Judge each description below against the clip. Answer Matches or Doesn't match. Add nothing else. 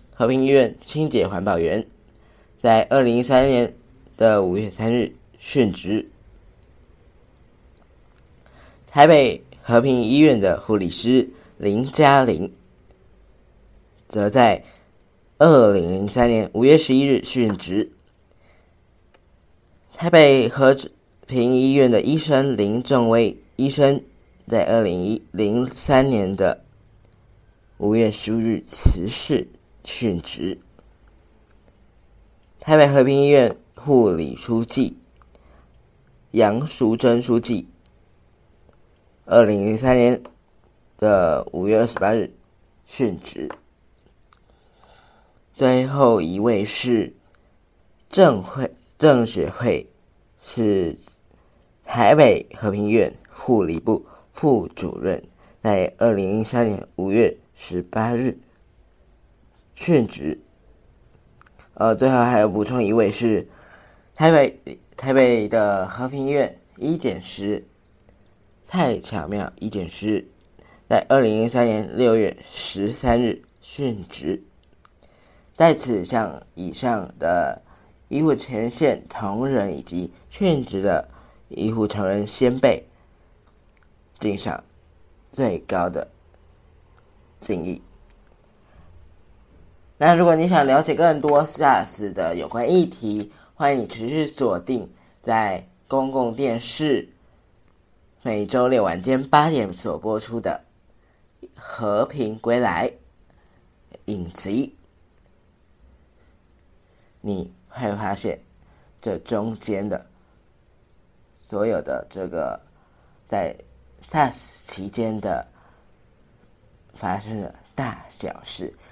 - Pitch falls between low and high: Doesn't match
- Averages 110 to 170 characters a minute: Matches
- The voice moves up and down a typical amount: Matches